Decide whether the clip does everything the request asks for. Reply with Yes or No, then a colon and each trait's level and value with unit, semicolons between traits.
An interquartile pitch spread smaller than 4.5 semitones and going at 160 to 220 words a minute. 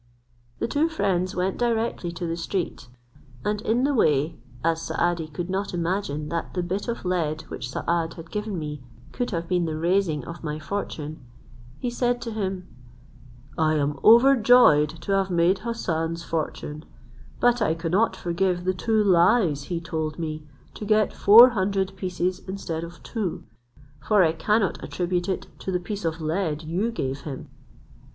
Yes: average, 3.9 semitones; average, 165 wpm